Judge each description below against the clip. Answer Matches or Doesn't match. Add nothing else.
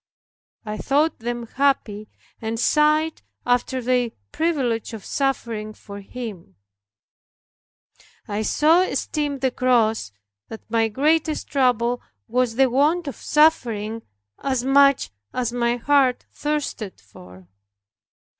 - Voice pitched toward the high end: Matches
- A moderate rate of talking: Doesn't match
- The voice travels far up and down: Doesn't match